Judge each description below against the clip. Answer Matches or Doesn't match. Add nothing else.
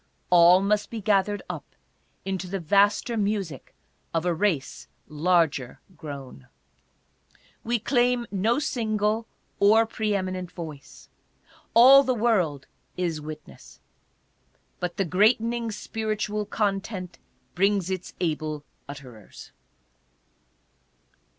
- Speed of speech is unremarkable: Doesn't match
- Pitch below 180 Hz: Doesn't match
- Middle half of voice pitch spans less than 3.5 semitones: Doesn't match